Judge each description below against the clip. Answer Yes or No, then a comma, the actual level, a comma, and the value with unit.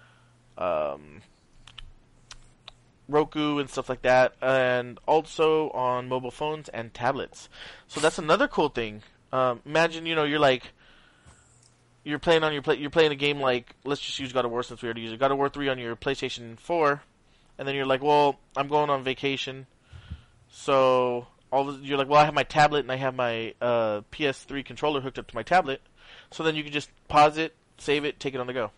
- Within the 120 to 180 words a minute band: No, fast, 205 wpm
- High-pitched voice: No, low, 135 Hz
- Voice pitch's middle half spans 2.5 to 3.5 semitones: Yes, average, 3.0 semitones